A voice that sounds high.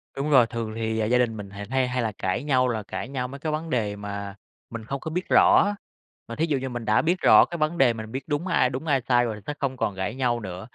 No: low, 125 Hz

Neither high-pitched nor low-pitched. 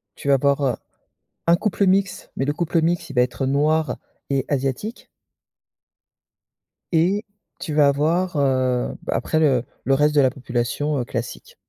Yes: medium, 145 Hz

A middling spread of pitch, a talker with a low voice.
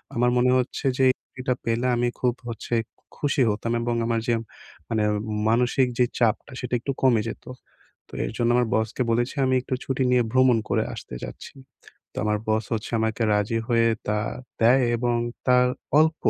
No: narrow, 1.8 semitones; low, 120 Hz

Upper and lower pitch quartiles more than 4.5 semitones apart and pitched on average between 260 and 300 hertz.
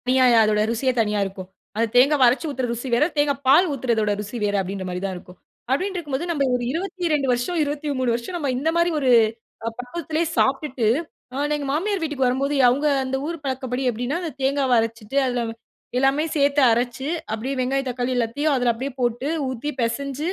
No: average, 3.4 semitones; very high, 265 Hz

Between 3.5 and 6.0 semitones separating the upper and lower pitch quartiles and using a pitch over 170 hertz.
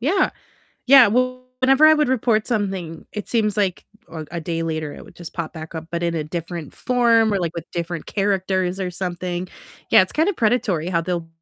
Yes: wide, 5.5 semitones; medium, 185 Hz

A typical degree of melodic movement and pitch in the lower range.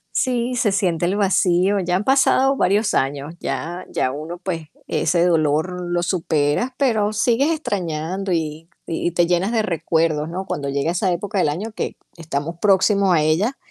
No: average, 4.2 semitones; medium, 180 Hz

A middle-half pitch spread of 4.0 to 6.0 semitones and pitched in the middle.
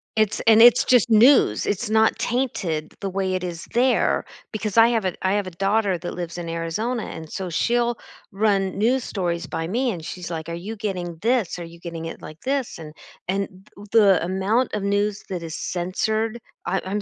No: average, 4.3 semitones; high, 195 Hz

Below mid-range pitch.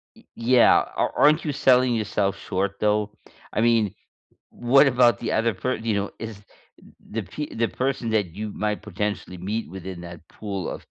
Yes: low, 110 Hz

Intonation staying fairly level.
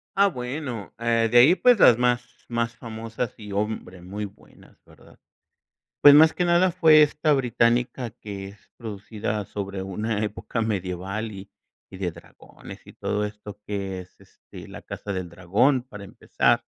No: average, 3.8 semitones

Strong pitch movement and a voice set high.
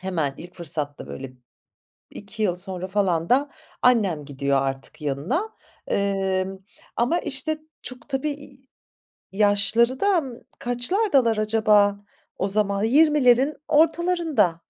Yes: wide, 6.8 semitones; high, 215 Hz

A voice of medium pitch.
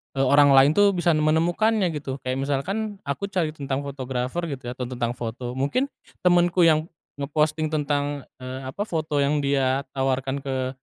Yes: medium, 145 Hz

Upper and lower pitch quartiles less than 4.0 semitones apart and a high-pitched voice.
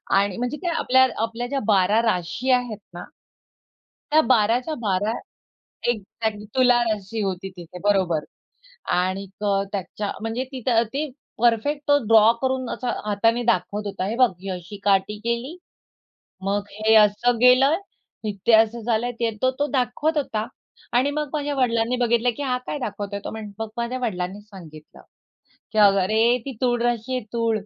Yes: average, 3.6 semitones; high, 230 Hz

